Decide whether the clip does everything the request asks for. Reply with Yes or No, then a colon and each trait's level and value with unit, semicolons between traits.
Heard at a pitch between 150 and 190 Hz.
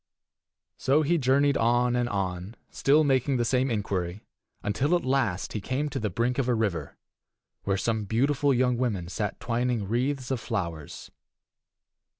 No: low, 120 Hz